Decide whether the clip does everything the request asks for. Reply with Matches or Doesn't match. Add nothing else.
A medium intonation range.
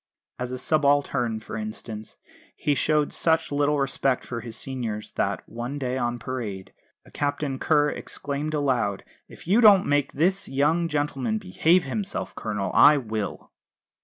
Matches